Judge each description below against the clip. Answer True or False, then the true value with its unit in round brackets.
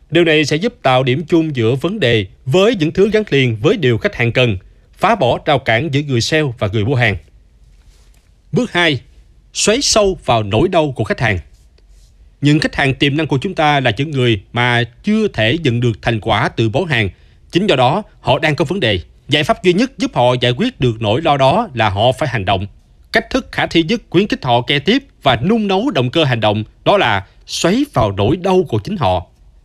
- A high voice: False (130 Hz)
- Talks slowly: False (230 wpm)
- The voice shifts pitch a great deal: True (7.0 semitones)